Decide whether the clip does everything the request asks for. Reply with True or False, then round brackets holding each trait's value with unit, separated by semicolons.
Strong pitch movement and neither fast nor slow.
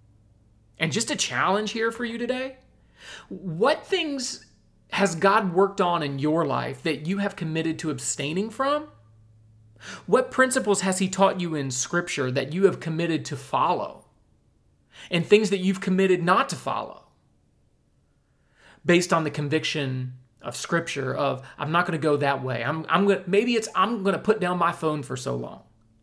True (5.9 semitones; 175 wpm)